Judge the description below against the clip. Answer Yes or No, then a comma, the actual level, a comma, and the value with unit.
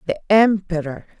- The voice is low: No, medium, 185 Hz